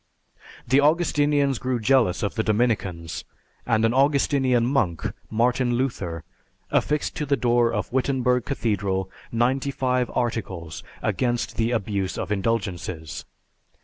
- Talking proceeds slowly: Yes, slow, 120 wpm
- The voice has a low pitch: Yes, low, 120 Hz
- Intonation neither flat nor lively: Yes, average, 4.5 semitones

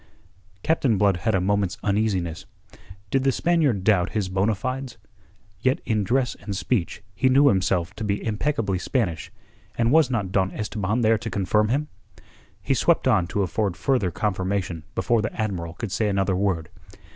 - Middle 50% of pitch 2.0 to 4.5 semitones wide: Yes, average, 4.0 semitones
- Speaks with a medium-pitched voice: No, low, 105 Hz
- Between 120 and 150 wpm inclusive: No, average, 170 wpm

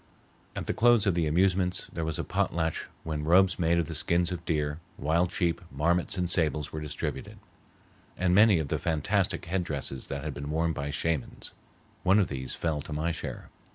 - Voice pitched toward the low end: Yes, very low, 80 Hz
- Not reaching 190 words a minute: No, average, 195 wpm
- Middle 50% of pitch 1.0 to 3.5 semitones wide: Yes, average, 2.9 semitones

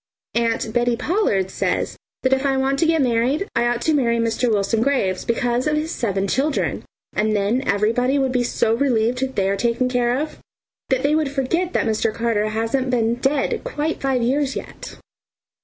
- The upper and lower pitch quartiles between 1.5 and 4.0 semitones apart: Yes, average, 3.2 semitones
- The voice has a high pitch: Yes, high, 245 Hz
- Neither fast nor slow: Yes, average, 190 wpm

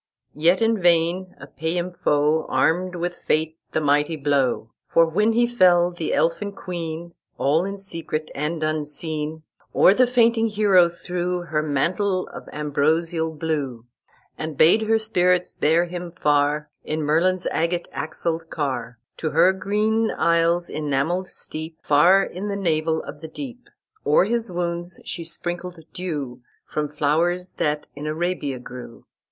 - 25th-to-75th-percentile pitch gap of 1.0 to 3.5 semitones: Yes, average, 3.0 semitones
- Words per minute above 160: No, average, 145 wpm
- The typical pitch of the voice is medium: Yes, medium, 170 Hz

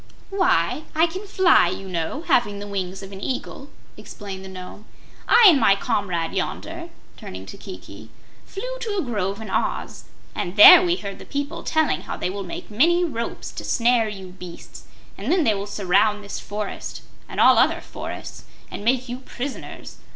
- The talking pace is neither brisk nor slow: Yes, average, 180 wpm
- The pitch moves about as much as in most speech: No, wide, 7.4 semitones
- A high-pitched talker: Yes, high, 210 Hz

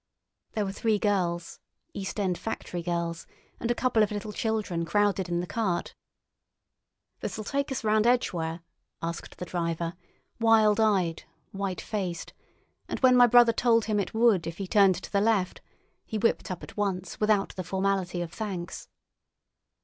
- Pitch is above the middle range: Yes, high, 200 Hz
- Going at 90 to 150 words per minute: No, average, 165 wpm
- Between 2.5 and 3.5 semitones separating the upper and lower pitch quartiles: No, average, 3.9 semitones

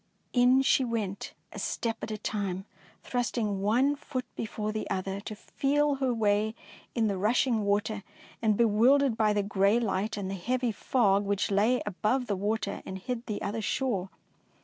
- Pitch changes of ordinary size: Yes, average, 3.4 semitones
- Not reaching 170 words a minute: No, average, 180 wpm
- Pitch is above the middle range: Yes, high, 215 Hz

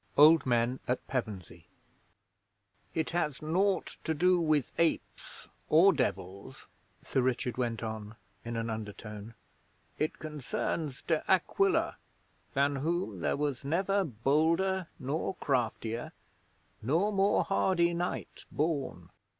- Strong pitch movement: Yes, wide, 6.5 semitones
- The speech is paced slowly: Yes, slow, 110 wpm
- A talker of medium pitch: Yes, medium, 145 Hz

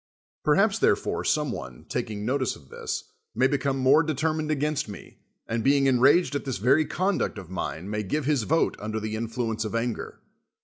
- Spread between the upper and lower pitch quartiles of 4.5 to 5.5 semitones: Yes, average, 4.9 semitones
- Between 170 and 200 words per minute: Yes, average, 185 wpm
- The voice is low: Yes, low, 130 Hz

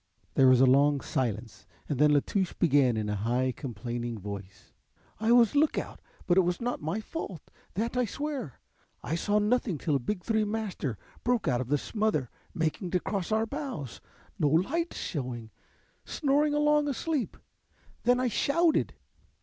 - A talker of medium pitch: Yes, medium, 180 Hz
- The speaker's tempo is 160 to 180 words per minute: Yes, average, 165 wpm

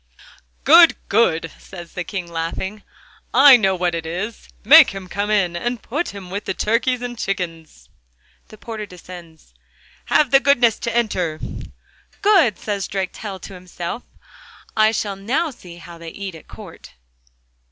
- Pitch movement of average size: Yes, average, 4.8 semitones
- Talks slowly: No, average, 150 wpm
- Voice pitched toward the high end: Yes, high, 195 Hz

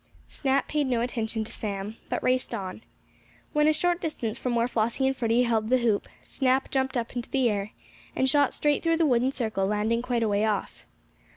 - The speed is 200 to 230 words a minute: Yes, fast, 205 wpm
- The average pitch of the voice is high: Yes, high, 240 Hz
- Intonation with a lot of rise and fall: No, average, 3.3 semitones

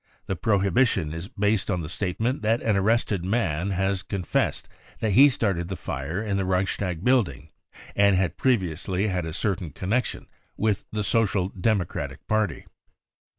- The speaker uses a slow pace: No, average, 155 wpm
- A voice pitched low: Yes, very low, 95 Hz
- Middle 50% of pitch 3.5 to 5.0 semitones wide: No, average, 3.1 semitones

